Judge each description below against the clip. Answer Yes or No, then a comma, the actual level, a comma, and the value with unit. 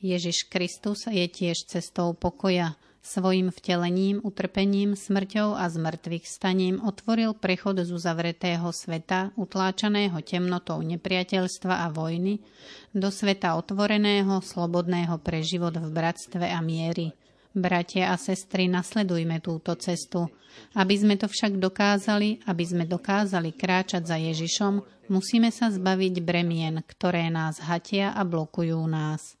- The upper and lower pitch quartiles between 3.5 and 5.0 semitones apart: No, narrow, 2.6 semitones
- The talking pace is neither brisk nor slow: Yes, average, 120 wpm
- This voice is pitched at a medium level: Yes, medium, 180 Hz